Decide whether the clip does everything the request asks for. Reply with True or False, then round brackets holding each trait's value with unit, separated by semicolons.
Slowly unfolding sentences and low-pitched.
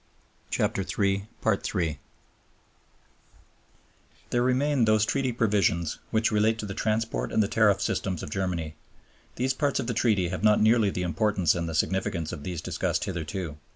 False (150 wpm; 105 Hz)